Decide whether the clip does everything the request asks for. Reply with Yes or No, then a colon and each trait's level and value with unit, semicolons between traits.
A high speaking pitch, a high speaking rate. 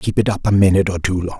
No: very low, 95 Hz; fast, 345 wpm